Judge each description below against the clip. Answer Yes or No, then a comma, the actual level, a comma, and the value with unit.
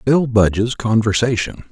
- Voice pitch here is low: Yes, low, 115 Hz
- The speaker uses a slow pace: Yes, slow, 105 wpm